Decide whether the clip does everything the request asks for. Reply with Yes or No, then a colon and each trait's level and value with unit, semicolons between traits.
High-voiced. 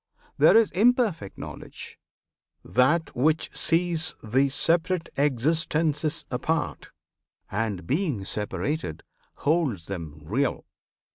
No: medium, 150 Hz